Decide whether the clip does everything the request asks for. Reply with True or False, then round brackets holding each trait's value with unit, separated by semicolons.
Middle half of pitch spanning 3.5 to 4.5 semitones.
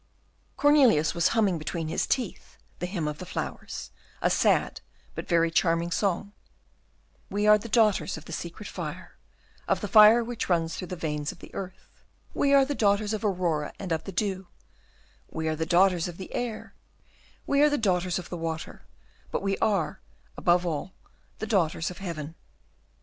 True (4.2 semitones)